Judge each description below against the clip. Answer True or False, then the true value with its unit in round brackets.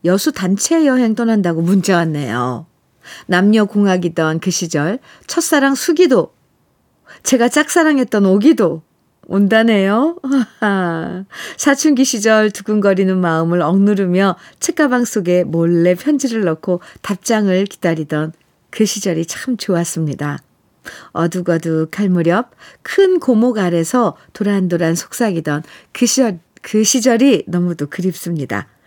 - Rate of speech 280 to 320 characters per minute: False (260 characters per minute)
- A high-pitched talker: True (195 Hz)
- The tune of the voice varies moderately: False (6.0 semitones)